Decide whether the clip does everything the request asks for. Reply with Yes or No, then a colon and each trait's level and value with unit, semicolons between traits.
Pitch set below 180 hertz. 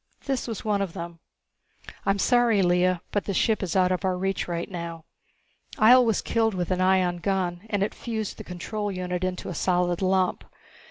No: medium, 185 Hz